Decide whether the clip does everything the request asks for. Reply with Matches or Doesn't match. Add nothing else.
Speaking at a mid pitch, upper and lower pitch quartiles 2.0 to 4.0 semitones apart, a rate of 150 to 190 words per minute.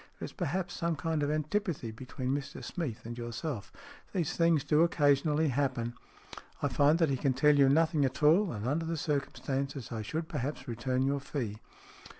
Matches